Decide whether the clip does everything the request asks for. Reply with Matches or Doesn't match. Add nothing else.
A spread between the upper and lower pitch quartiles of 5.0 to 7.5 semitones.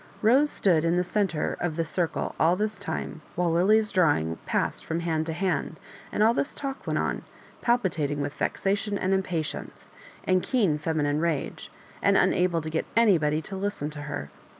Doesn't match